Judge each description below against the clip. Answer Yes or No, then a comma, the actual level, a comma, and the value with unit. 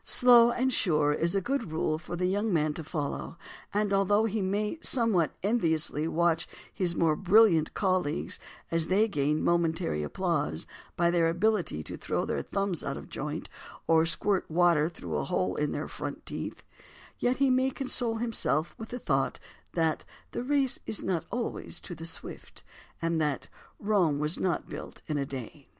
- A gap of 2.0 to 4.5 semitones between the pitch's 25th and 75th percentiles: No, average, 5.3 semitones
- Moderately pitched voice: Yes, medium, 175 Hz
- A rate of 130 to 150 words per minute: No, average, 175 wpm